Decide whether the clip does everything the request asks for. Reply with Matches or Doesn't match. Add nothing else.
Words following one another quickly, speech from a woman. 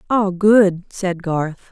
Doesn't match